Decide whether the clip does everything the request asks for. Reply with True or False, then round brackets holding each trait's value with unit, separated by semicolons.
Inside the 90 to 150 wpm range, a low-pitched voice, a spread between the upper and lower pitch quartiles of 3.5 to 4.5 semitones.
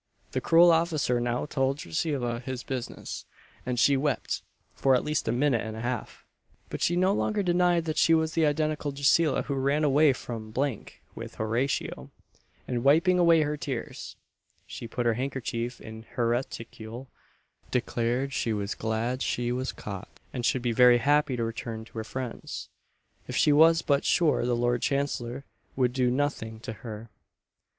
False (170 wpm; 130 Hz; 3.9 semitones)